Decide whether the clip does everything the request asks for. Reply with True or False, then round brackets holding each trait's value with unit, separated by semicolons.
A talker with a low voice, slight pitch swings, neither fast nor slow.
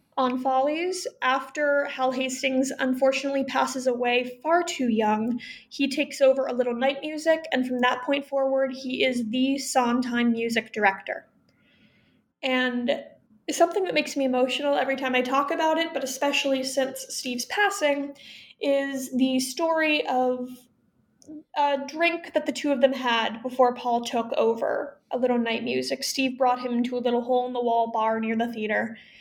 False (260 Hz; 2.3 semitones; 165 wpm)